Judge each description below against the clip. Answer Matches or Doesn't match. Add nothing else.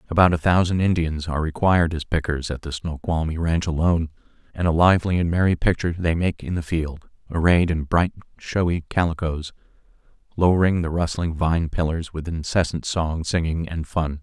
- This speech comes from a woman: Doesn't match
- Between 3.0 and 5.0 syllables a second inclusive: Doesn't match